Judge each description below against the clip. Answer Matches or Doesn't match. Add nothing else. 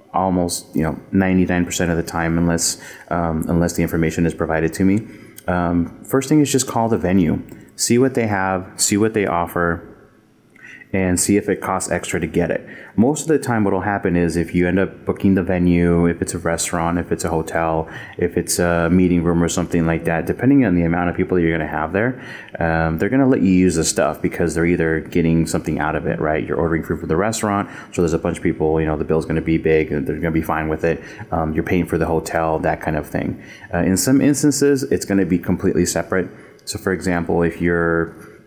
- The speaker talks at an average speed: Doesn't match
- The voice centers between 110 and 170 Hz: Doesn't match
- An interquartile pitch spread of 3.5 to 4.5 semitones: Doesn't match